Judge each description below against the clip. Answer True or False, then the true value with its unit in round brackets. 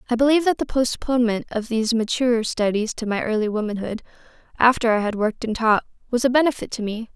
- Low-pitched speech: False (230 Hz)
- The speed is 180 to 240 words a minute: True (200 wpm)